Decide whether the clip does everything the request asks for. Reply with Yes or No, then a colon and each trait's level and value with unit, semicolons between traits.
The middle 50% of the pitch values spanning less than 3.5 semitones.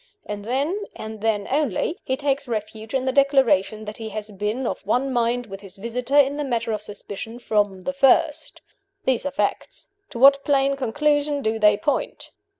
No: average, 4.5 semitones